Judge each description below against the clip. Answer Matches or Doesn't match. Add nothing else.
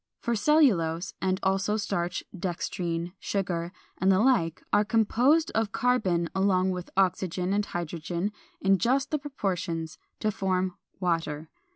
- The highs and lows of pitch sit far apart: Doesn't match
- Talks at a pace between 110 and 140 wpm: Matches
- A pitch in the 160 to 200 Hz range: Matches